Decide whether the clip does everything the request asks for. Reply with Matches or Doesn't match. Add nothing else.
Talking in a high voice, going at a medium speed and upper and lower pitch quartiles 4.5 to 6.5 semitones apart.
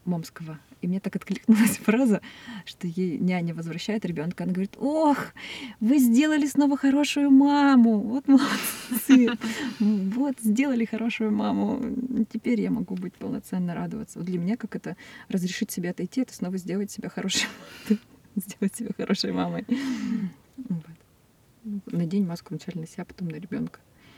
Matches